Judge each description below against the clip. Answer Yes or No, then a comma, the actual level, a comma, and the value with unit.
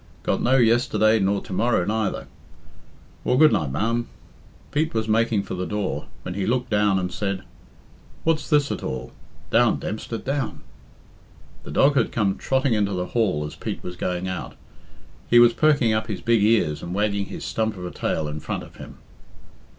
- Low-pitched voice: Yes, low, 110 Hz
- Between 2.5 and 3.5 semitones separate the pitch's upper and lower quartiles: No, average, 3.9 semitones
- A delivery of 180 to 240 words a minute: Yes, average, 185 wpm